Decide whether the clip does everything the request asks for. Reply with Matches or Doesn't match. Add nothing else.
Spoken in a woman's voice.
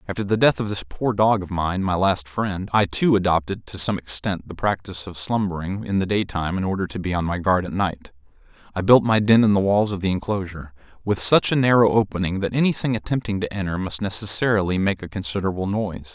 Doesn't match